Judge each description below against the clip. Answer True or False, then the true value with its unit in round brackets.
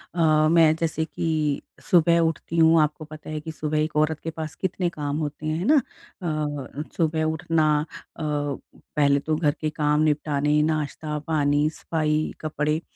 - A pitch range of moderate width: False (1.2 semitones)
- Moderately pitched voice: True (155 Hz)